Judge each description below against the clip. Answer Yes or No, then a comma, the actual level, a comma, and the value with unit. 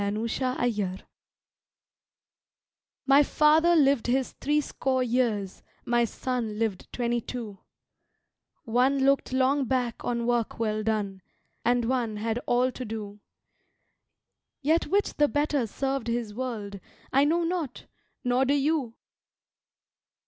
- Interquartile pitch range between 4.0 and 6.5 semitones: No, average, 3.5 semitones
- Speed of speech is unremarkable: No, slow, 125 wpm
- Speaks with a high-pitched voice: Yes, high, 245 Hz